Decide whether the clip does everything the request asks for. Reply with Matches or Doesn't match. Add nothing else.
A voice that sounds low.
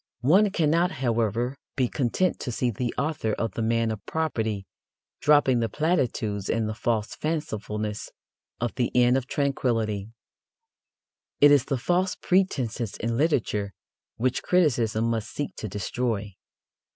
Matches